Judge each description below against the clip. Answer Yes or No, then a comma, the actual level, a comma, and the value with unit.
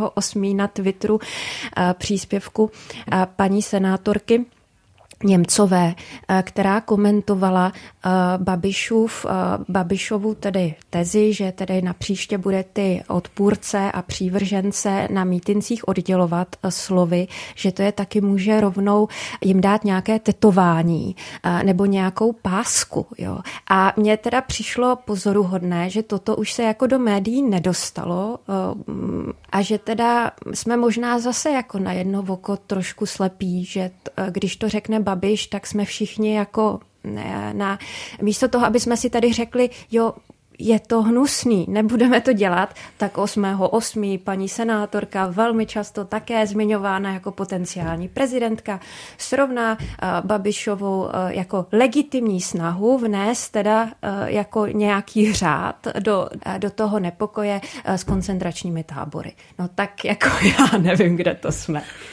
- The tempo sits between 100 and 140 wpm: Yes, average, 125 wpm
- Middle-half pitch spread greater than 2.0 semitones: Yes, narrow, 2.4 semitones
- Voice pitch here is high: Yes, high, 200 Hz